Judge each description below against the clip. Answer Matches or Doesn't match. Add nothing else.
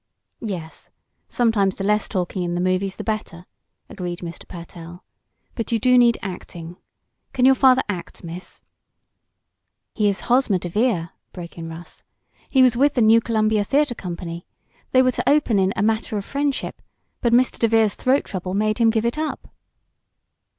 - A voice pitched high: Matches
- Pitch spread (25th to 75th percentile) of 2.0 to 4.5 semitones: Doesn't match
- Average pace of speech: Matches